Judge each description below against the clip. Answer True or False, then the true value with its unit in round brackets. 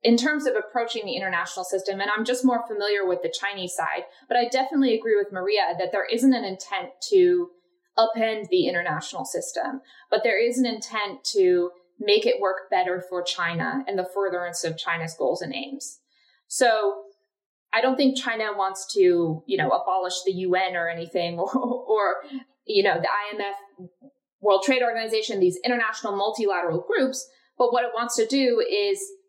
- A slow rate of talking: False (175 wpm)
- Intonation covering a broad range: True (5.8 semitones)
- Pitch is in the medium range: False (215 Hz)